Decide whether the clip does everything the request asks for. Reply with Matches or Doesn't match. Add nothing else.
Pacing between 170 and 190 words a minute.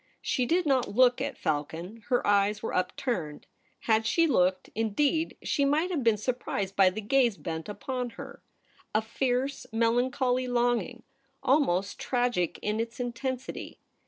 Doesn't match